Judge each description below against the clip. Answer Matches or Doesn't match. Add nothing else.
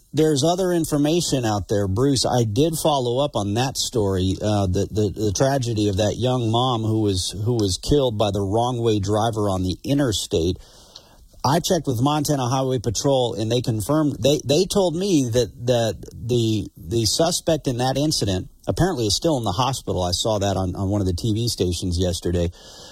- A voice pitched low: Matches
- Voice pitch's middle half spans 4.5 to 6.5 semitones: Matches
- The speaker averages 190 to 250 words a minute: Matches